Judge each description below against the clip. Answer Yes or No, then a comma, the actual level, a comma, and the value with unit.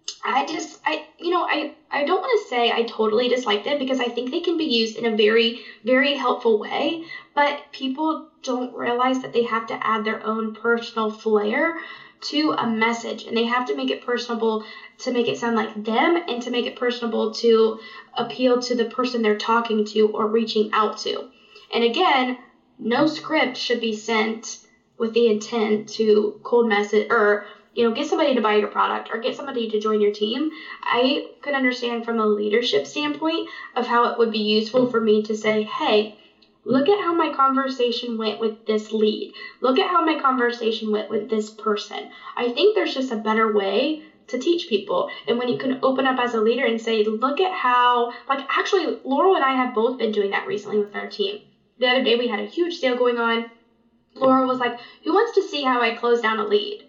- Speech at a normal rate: No, fast, 210 wpm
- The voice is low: No, high, 235 Hz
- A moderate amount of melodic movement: Yes, average, 3.3 semitones